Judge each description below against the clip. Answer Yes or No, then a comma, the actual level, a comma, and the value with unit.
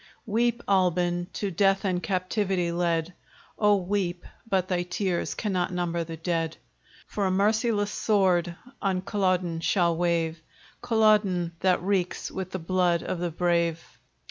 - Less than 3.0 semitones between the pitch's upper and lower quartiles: Yes, narrow, 2.4 semitones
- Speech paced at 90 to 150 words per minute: Yes, average, 140 wpm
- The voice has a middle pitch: Yes, medium, 180 Hz